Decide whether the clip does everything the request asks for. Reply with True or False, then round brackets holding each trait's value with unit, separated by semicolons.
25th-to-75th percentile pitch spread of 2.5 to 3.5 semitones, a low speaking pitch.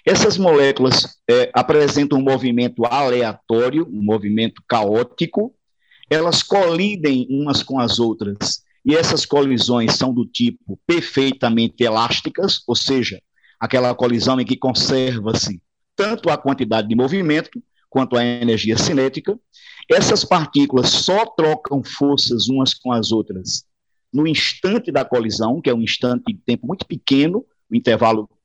False (4.5 semitones; 130 Hz)